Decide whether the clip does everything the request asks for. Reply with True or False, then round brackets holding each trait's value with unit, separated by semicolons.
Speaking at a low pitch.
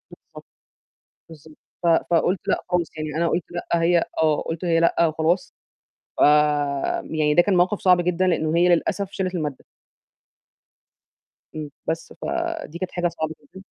False (170 Hz)